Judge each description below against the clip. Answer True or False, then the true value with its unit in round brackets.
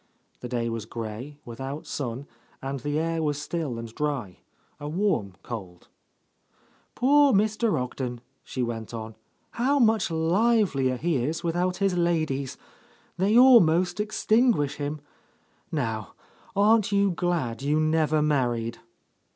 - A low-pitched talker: False (150 Hz)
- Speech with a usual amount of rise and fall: False (7.4 semitones)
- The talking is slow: True (130 wpm)